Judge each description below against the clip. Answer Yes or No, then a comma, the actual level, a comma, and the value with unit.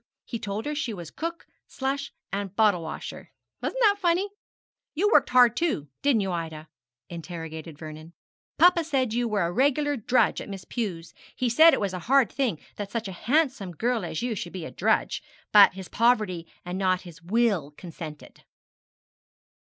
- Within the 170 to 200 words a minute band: Yes, average, 175 wpm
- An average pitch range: No, wide, 7.3 semitones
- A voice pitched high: Yes, high, 210 Hz